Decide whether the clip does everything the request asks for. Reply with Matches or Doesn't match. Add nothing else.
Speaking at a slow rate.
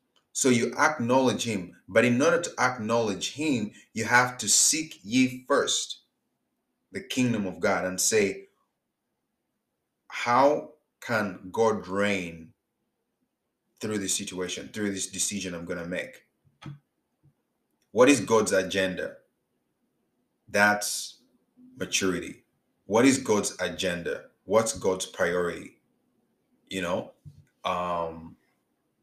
Matches